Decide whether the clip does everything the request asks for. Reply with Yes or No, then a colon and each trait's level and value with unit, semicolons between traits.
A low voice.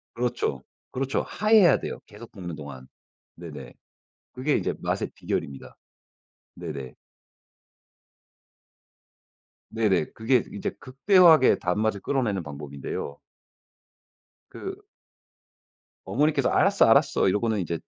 Yes: low, 110 Hz